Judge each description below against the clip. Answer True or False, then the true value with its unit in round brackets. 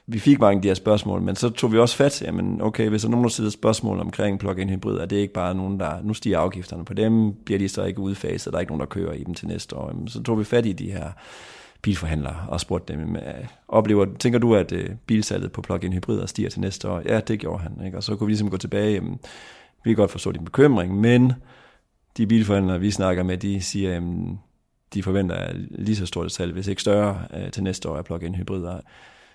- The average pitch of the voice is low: True (100 Hz)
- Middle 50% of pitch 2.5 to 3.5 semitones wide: True (3.2 semitones)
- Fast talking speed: True (245 wpm)